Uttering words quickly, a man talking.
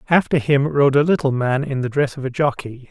Yes: fast, 250 wpm; male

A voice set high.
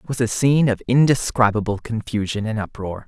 No: low, 115 Hz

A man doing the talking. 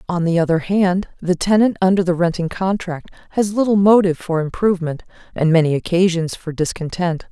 No: female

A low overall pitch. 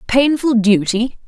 No: high, 240 Hz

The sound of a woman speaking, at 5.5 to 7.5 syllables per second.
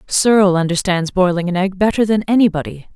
Yes: female; 5.8 syllables/s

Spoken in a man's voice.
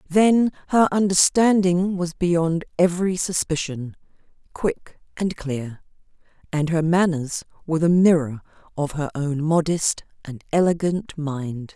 No: female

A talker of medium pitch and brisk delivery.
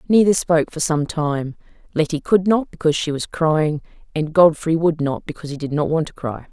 Yes: medium, 160 Hz; fast, 210 wpm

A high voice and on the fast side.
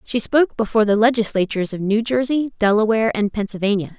No: high, 220 Hz; average, 165 wpm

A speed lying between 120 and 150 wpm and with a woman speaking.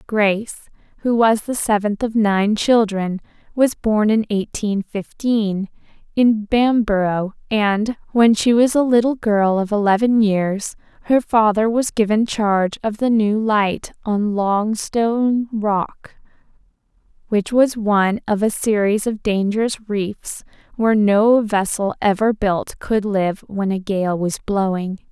Yes: average, 140 wpm; female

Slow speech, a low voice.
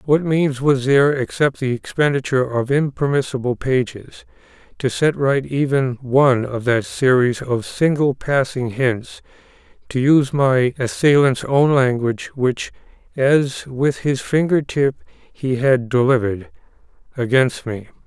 Yes: slow, 130 wpm; low, 130 Hz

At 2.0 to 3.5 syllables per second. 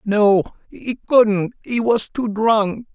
Yes: 3.0 syllables/s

